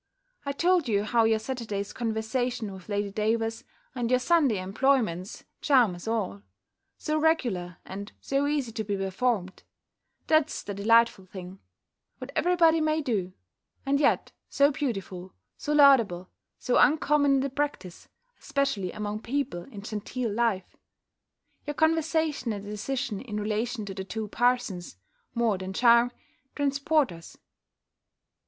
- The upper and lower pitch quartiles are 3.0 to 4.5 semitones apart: No, wide, 5.6 semitones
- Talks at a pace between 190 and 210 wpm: No, average, 140 wpm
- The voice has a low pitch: No, high, 230 Hz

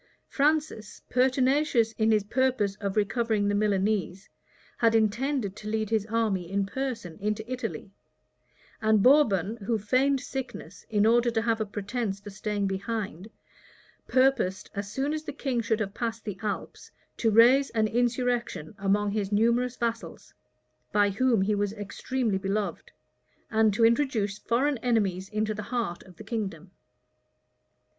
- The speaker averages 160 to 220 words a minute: No, average, 150 wpm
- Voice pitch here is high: Yes, high, 220 Hz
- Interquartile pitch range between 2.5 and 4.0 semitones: Yes, average, 3.1 semitones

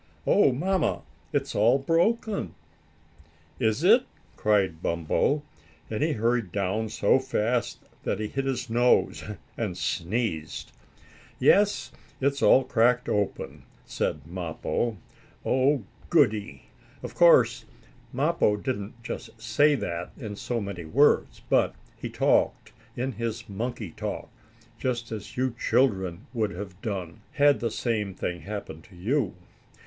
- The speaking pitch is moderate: No, low, 115 Hz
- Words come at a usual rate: No, slow, 125 wpm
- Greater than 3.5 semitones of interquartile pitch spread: Yes, average, 4.8 semitones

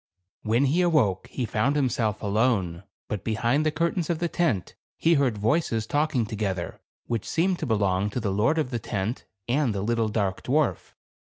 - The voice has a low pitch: Yes, low, 115 Hz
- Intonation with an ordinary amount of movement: No, wide, 6.1 semitones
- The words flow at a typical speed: Yes, average, 180 wpm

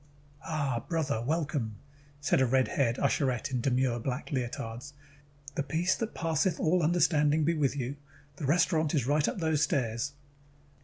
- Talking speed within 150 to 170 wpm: Yes, average, 155 wpm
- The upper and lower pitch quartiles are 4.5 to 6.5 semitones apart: No, average, 3.7 semitones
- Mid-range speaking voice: Yes, medium, 145 Hz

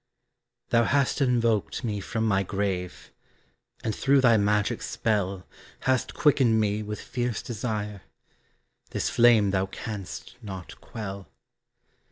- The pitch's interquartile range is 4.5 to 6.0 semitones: No, average, 3.1 semitones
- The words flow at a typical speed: No, slow, 120 wpm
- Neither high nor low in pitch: No, low, 105 Hz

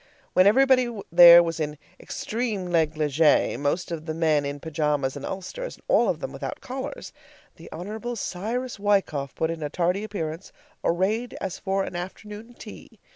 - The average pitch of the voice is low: No, medium, 180 Hz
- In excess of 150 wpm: Yes, average, 165 wpm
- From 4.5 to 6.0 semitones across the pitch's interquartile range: Yes, wide, 5.4 semitones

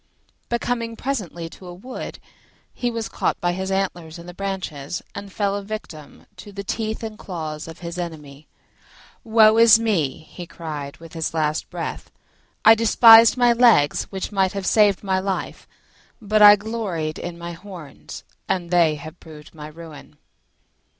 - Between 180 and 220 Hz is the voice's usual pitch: Yes, medium, 185 Hz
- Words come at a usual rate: Yes, average, 165 wpm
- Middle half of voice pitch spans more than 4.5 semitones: Yes, average, 4.9 semitones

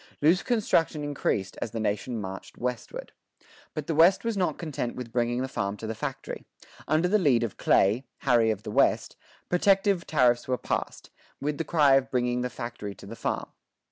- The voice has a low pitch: Yes, low, 125 Hz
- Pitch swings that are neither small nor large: No, wide, 6.2 semitones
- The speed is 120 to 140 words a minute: No, average, 190 wpm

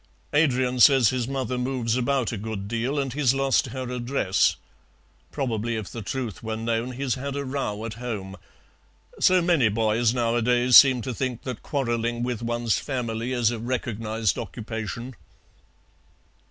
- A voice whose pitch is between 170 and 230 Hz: No, low, 120 Hz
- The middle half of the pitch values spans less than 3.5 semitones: Yes, narrow, 2.4 semitones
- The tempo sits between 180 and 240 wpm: No, average, 155 wpm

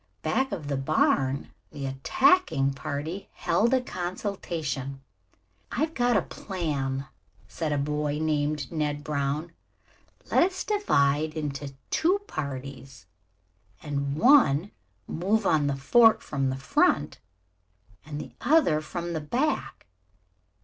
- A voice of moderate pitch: Yes, medium, 150 Hz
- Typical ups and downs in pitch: No, wide, 6.2 semitones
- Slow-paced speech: Yes, slow, 120 wpm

